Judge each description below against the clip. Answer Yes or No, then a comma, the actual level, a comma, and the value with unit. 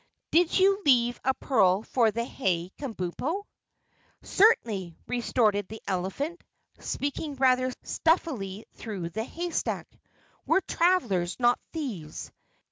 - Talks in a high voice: Yes, high, 240 Hz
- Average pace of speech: No, slow, 110 wpm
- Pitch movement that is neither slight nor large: No, wide, 7.7 semitones